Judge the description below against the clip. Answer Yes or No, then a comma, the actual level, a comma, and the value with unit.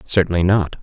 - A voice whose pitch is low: Yes, very low, 90 Hz